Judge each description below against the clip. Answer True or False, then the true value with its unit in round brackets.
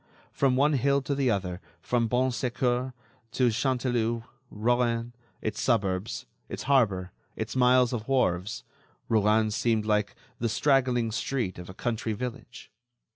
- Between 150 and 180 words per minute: False (135 wpm)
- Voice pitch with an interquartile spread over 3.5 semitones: False (3.0 semitones)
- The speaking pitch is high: False (120 Hz)